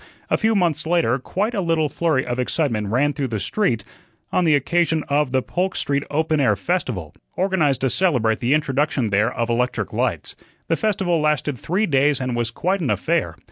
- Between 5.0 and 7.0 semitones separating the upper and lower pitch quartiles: Yes, wide, 5.5 semitones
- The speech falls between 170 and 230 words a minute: Yes, average, 190 wpm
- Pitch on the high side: No, medium, 145 Hz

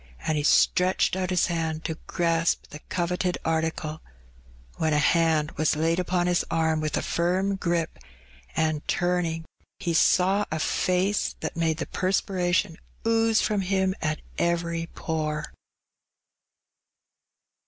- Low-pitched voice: No, medium, 170 Hz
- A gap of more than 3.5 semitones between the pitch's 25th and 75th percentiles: No, narrow, 2.4 semitones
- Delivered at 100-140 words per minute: Yes, slow, 135 wpm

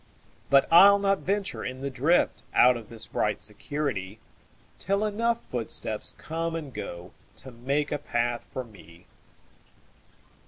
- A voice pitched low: Yes, low, 130 Hz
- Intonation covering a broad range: Yes, wide, 6.8 semitones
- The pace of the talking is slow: Yes, slow, 120 wpm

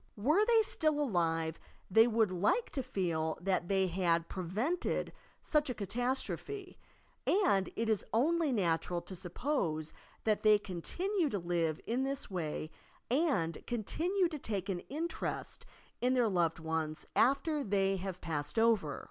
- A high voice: Yes, high, 205 Hz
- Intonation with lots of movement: Yes, wide, 8.2 semitones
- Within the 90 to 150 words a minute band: Yes, average, 145 wpm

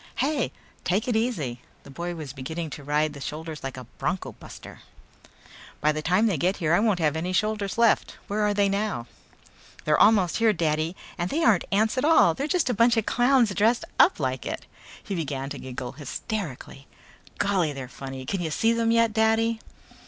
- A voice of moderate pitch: Yes, medium, 180 Hz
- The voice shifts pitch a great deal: Yes, wide, 6.8 semitones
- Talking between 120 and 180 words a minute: No, average, 195 wpm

